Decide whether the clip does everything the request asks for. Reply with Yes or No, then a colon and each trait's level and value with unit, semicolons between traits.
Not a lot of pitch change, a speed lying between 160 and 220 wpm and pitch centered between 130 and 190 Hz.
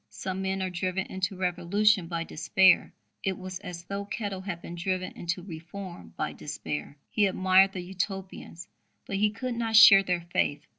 Yes: narrow, 2.0 semitones; average, 170 wpm; medium, 185 Hz